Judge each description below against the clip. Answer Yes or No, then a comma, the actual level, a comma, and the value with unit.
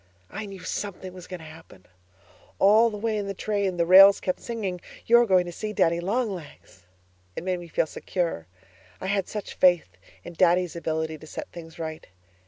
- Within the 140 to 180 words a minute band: No, average, 190 wpm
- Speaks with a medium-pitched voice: Yes, medium, 180 Hz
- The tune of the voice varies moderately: Yes, average, 3.3 semitones